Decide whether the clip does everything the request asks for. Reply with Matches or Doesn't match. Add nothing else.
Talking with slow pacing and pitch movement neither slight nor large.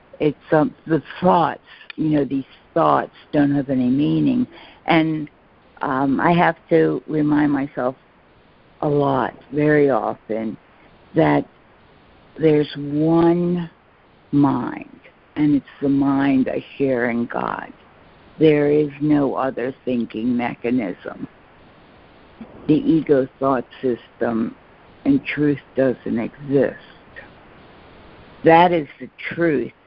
Matches